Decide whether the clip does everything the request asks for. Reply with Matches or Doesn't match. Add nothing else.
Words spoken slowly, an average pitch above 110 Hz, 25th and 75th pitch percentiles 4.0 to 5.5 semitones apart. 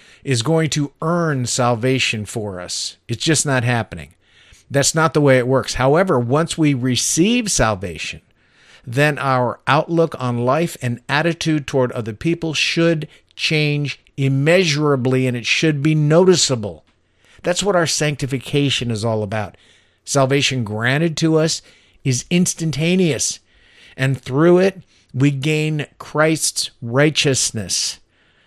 Matches